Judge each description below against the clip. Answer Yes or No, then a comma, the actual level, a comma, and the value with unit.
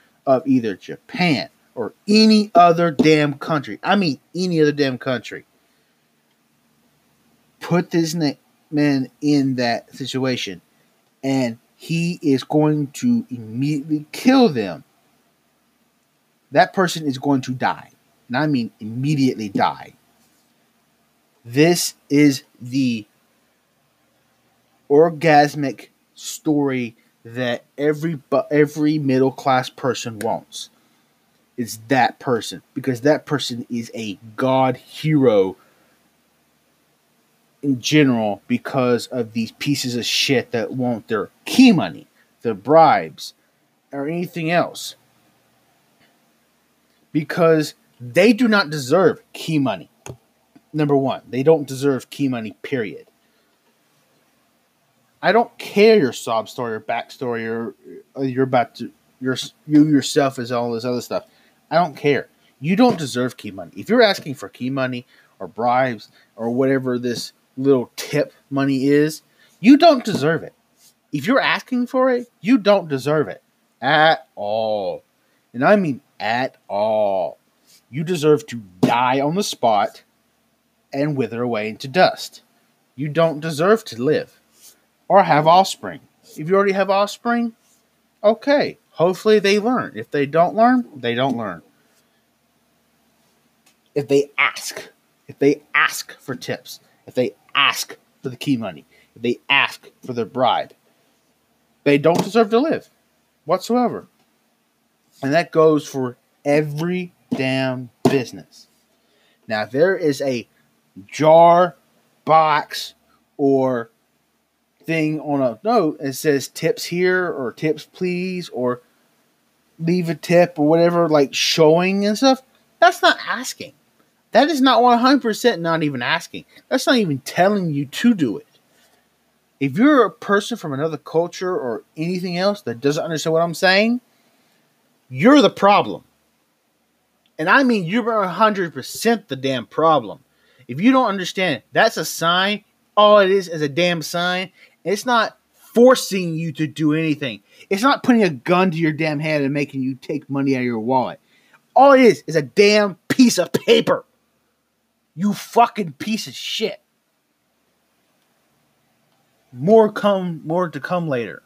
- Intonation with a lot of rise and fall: Yes, wide, 6.8 semitones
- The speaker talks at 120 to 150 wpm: Yes, slow, 135 wpm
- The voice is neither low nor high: Yes, medium, 155 Hz